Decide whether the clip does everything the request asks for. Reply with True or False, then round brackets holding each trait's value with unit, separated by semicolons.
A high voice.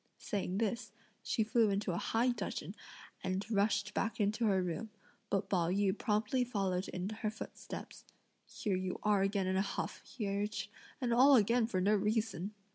True (205 Hz)